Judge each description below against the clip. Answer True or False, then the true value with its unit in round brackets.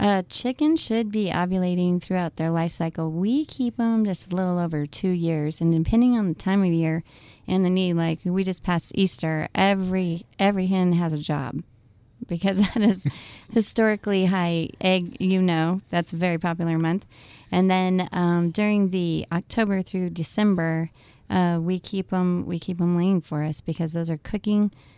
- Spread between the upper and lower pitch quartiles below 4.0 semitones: True (2.8 semitones)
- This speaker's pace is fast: False (180 wpm)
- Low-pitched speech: False (180 Hz)